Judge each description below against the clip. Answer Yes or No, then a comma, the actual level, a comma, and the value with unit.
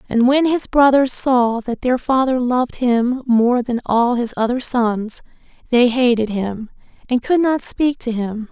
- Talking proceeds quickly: No, average, 175 wpm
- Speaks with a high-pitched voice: Yes, high, 245 Hz